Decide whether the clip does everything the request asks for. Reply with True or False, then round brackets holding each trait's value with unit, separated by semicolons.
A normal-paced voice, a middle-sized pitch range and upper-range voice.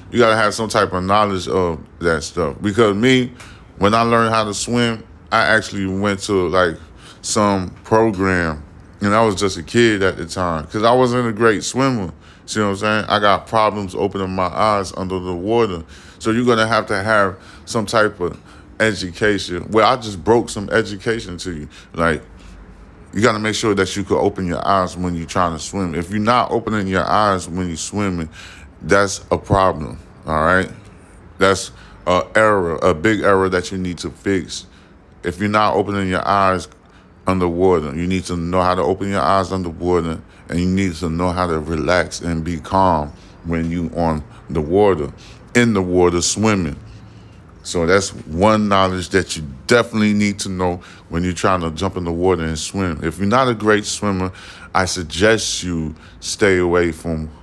False (190 wpm; 3.2 semitones; 95 Hz)